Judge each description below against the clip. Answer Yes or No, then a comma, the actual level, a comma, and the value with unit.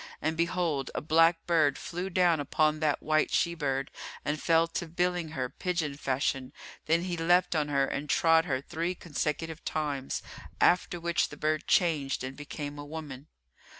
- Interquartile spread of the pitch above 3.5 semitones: No, average, 2.8 semitones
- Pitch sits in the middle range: Yes, medium, 155 Hz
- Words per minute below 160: No, average, 170 wpm